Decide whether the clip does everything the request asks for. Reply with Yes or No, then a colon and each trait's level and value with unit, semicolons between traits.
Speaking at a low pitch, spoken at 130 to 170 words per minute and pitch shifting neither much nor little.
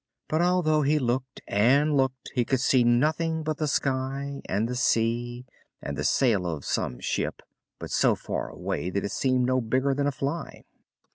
No: low, 130 Hz; average, 185 wpm; average, 3.2 semitones